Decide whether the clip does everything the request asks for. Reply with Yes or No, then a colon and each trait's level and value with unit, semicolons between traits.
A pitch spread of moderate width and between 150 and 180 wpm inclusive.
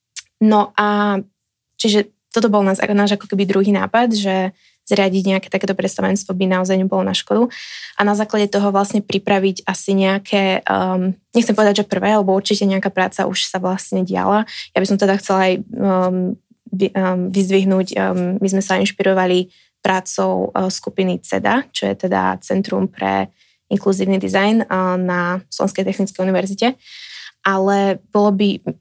No: narrow, 1.4 semitones; average, 155 wpm